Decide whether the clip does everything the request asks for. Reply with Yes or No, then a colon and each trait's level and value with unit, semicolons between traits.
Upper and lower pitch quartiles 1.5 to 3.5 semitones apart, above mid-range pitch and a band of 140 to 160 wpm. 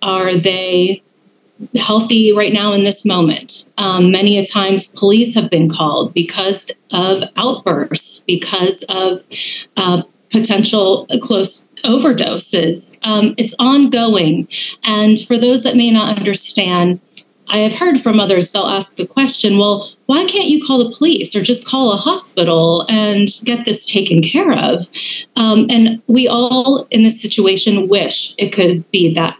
No: average, 3.9 semitones; high, 210 Hz; average, 150 wpm